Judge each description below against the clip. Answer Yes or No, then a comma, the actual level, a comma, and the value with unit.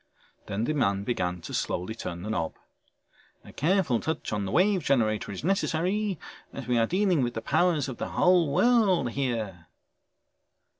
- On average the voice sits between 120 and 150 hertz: Yes, low, 135 Hz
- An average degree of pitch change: No, wide, 8.8 semitones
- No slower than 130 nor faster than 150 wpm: No, average, 165 wpm